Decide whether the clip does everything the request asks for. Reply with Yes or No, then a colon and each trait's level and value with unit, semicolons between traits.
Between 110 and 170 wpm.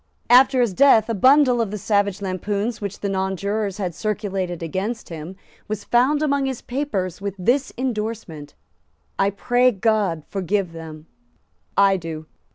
Yes: average, 150 wpm